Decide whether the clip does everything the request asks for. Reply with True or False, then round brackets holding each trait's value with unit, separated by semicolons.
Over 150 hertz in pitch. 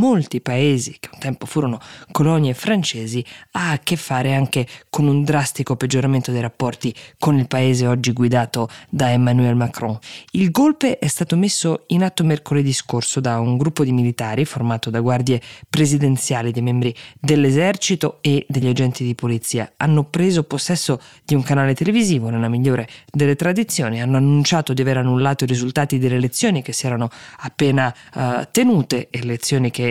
False (135 Hz)